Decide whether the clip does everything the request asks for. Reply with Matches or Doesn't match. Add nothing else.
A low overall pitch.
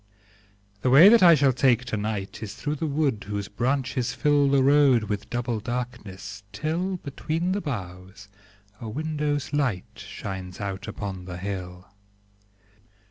Matches